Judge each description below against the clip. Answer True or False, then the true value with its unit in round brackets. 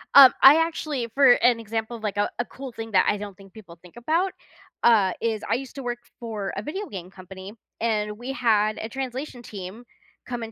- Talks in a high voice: True (230 Hz)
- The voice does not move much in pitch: False (3.7 semitones)